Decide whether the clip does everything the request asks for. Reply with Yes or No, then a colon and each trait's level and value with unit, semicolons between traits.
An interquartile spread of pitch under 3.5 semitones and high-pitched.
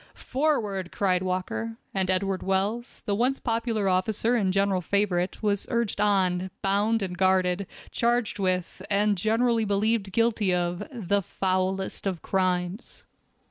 Yes: average, 3.0 semitones; high, 195 Hz